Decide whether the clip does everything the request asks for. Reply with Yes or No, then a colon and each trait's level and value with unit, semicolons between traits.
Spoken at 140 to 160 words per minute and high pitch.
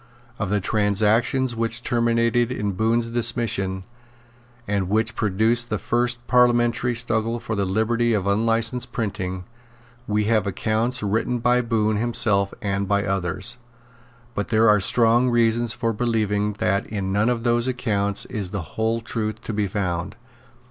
No: average, 150 wpm; low, 110 Hz